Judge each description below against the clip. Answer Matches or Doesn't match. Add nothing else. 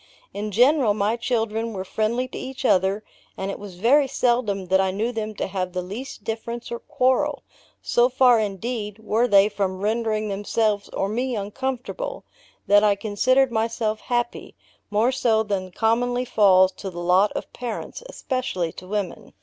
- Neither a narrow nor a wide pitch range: Matches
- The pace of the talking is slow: Doesn't match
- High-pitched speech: Matches